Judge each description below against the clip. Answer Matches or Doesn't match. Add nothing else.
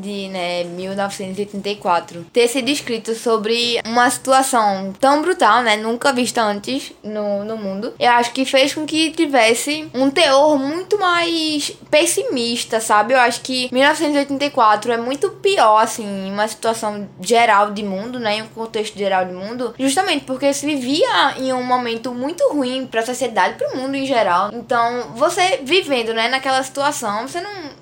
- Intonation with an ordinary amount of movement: Matches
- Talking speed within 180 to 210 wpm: Doesn't match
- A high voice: Matches